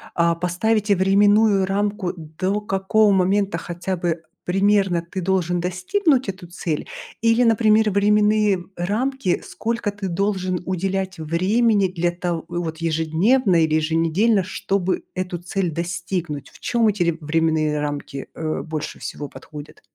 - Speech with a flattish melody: No, average, 3.4 semitones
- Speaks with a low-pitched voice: No, medium, 185 Hz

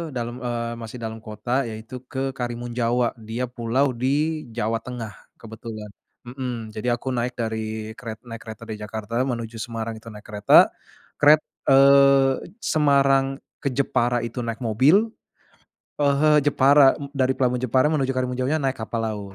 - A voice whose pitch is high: No, low, 120 Hz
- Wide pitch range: No, average, 3.0 semitones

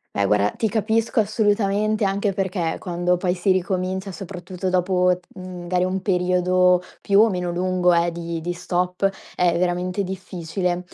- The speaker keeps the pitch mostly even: Yes, narrow, 1.6 semitones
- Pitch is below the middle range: No, medium, 180 Hz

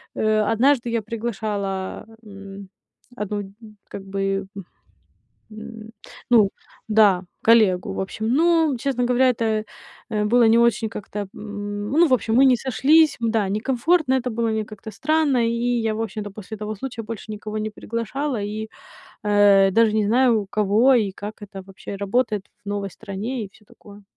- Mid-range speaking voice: No, high, 220 Hz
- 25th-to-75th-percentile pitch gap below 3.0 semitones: Yes, narrow, 2.6 semitones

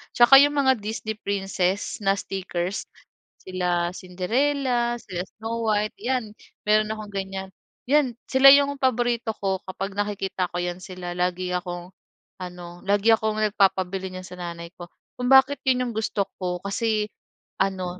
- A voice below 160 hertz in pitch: No, high, 200 Hz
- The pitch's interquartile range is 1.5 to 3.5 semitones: No, average, 4.1 semitones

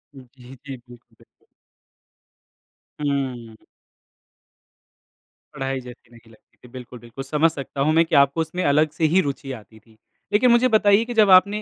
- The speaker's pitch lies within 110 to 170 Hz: Yes, medium, 140 Hz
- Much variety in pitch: No, average, 5.0 semitones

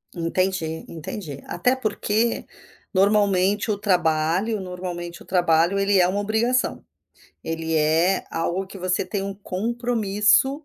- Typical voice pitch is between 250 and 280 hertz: No, high, 190 Hz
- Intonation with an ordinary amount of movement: Yes, average, 3.3 semitones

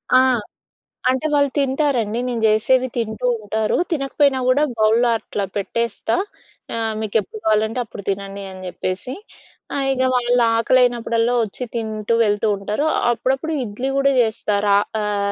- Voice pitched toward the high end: Yes, high, 230 Hz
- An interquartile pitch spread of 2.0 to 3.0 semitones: No, average, 3.4 semitones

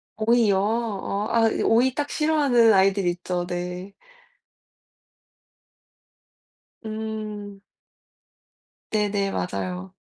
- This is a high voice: Yes, high, 205 Hz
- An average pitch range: Yes, average, 3.4 semitones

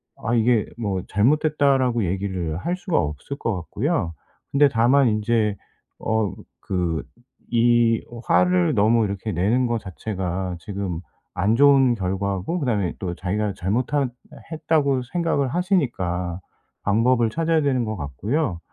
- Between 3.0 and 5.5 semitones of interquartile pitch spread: No, wide, 6.1 semitones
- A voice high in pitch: No, low, 110 Hz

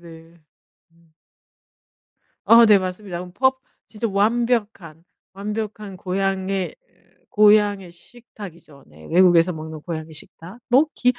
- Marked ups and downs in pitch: No, average, 4.1 semitones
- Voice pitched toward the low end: No, high, 190 Hz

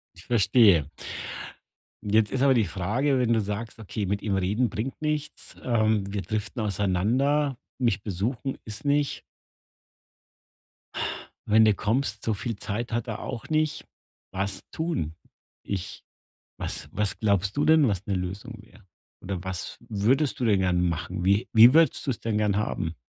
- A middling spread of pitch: Yes, average, 4.1 semitones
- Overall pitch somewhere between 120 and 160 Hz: No, low, 110 Hz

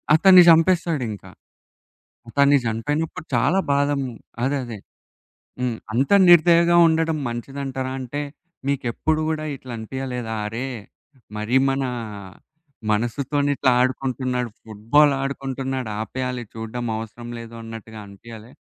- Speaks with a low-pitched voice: Yes, low, 130 Hz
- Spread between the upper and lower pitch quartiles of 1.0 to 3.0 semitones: No, average, 3.8 semitones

